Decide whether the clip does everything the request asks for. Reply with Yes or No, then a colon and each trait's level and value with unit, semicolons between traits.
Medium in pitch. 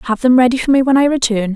No: high, 245 Hz